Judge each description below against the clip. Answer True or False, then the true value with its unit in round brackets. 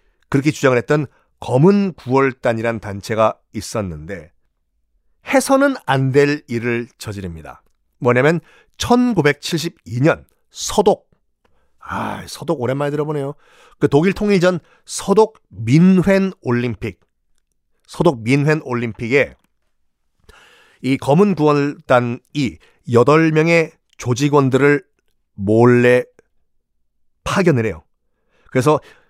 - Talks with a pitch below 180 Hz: True (135 Hz)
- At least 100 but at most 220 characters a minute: True (200 characters per minute)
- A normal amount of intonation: False (6.5 semitones)